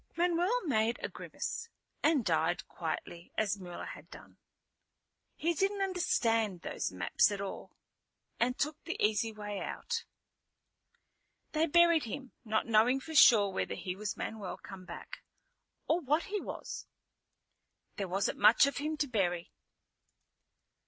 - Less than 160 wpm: Yes, average, 140 wpm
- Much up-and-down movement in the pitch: Yes, wide, 8.2 semitones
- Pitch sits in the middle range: No, high, 230 Hz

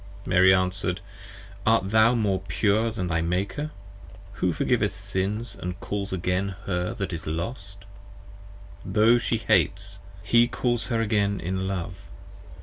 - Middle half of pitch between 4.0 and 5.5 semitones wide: No, average, 3.0 semitones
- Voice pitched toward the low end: Yes, low, 100 Hz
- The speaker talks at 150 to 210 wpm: No, slow, 135 wpm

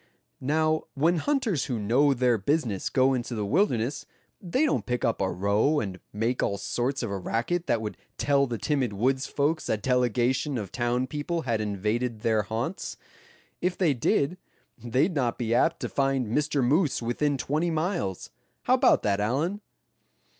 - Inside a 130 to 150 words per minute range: No, average, 170 wpm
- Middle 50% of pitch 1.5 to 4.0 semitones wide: No, average, 4.8 semitones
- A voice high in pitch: No, low, 125 Hz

